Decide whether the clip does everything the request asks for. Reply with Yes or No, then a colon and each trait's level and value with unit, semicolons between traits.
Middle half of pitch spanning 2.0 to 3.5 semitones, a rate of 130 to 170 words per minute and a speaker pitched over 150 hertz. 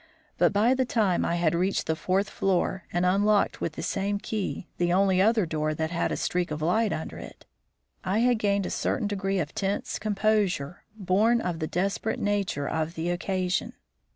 No: average, 3.0 semitones; average, 190 wpm; high, 190 Hz